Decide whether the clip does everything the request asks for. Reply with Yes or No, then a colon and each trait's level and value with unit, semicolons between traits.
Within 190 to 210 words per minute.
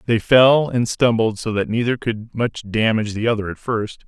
Yes: fast, 205 wpm